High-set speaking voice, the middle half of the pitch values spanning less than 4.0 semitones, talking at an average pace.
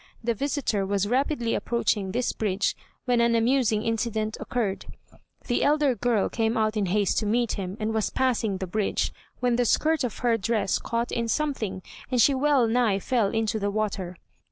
Yes: high, 225 Hz; average, 2.9 semitones; average, 180 wpm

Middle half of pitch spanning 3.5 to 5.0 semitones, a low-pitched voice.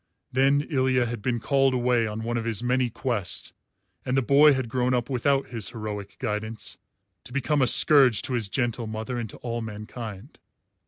No: average, 2.8 semitones; low, 120 Hz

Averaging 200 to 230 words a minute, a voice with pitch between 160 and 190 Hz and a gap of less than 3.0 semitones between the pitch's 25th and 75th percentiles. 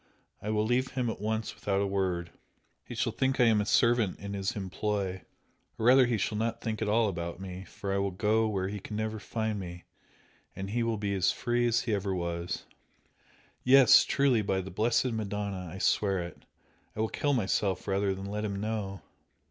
No: fast, 205 wpm; low, 105 Hz; narrow, 2.6 semitones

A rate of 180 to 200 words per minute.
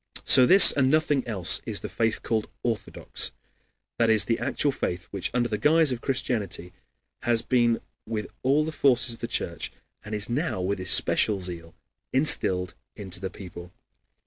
No: average, 170 wpm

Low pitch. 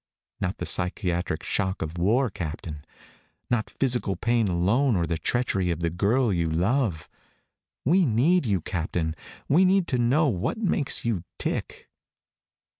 Yes: low, 100 Hz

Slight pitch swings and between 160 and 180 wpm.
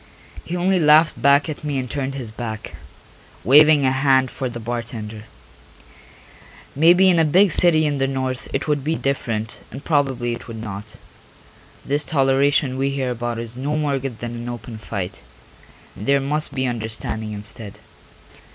No: average, 3.7 semitones; average, 170 wpm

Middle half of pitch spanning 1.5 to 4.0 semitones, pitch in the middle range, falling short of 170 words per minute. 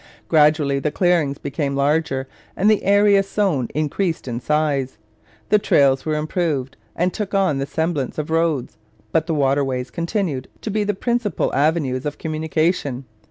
No: average, 4.4 semitones; medium, 155 Hz; average, 155 wpm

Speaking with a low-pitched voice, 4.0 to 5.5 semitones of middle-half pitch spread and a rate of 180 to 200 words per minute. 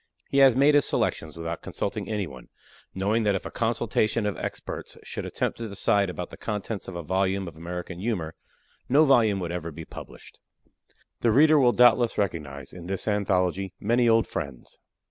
Yes: low, 100 Hz; average, 4.7 semitones; average, 185 wpm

